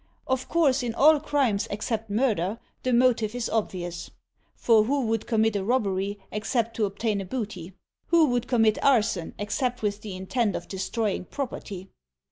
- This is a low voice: No, high, 220 Hz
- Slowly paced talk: No, average, 160 wpm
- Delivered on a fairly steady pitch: No, average, 3.6 semitones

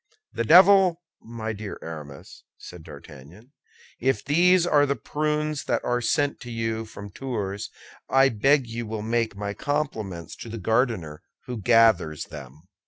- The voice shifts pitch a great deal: Yes, wide, 5.8 semitones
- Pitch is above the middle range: No, low, 115 Hz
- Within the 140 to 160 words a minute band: Yes, average, 150 wpm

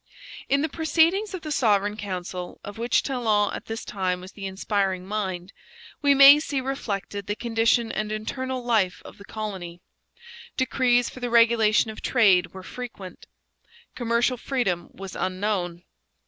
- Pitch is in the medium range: No, high, 215 Hz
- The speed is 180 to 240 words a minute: No, average, 150 wpm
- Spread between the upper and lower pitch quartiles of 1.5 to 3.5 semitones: No, average, 4.6 semitones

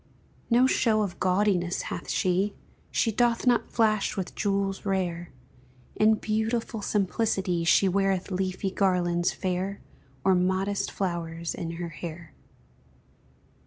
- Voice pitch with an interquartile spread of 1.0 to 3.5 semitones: Yes, average, 2.9 semitones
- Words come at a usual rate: No, slow, 120 wpm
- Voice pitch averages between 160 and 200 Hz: Yes, high, 190 Hz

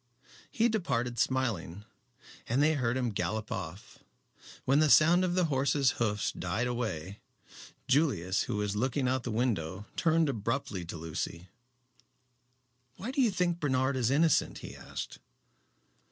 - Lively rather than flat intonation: Yes, wide, 6.2 semitones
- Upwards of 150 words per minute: No, average, 145 wpm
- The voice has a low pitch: Yes, low, 125 Hz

